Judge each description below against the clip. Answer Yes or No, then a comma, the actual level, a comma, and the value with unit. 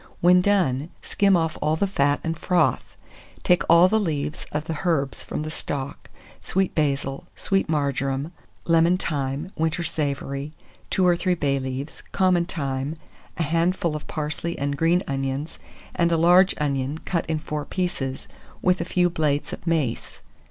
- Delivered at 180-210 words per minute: No, average, 160 wpm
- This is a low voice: No, medium, 160 Hz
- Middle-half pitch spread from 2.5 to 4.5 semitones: Yes, average, 3.8 semitones